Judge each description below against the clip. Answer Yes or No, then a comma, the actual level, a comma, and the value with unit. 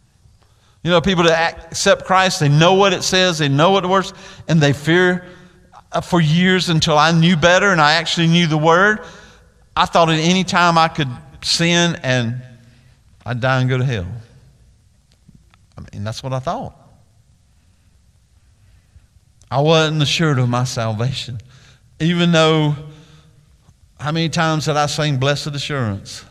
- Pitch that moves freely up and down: Yes, wide, 6.0 semitones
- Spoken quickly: No, average, 155 wpm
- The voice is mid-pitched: Yes, medium, 150 Hz